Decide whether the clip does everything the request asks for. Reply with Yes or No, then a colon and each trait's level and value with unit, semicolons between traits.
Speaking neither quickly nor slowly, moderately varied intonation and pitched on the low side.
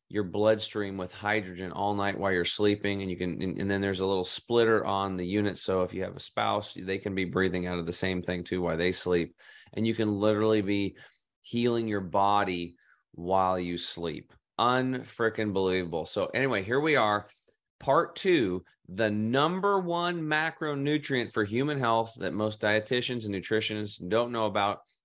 Yes: average, 180 wpm; average, 3.3 semitones; low, 105 Hz